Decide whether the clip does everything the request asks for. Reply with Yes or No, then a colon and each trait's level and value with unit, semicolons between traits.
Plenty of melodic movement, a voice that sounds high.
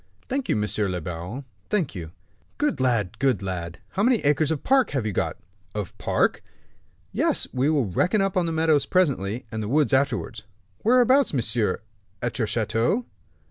No: wide, 8.5 semitones; low, 130 Hz